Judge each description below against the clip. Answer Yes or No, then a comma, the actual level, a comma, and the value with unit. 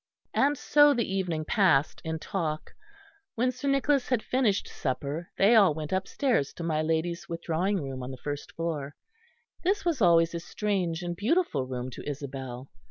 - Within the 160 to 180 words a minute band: Yes, average, 165 wpm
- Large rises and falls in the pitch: Yes, wide, 6.9 semitones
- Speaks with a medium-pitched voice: Yes, medium, 170 Hz